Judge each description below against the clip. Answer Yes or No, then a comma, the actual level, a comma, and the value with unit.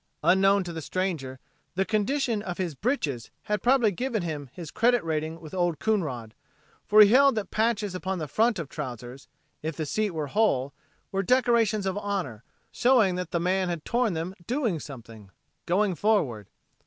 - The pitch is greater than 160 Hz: Yes, medium, 185 Hz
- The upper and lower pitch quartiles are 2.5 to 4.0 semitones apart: No, wide, 5.6 semitones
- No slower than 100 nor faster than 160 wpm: No, average, 170 wpm